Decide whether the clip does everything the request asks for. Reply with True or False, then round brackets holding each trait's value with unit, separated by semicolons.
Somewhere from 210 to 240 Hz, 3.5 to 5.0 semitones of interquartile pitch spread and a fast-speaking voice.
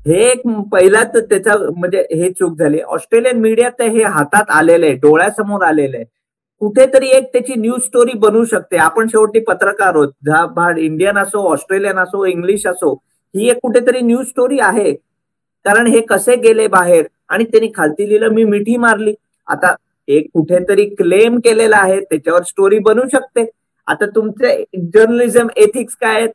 True (220 Hz; 4.4 semitones; 160 wpm)